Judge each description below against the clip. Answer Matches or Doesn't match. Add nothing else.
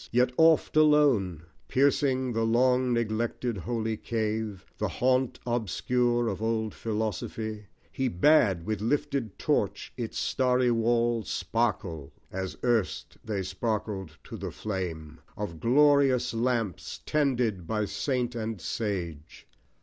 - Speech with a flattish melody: Doesn't match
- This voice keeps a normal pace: Doesn't match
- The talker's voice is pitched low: Matches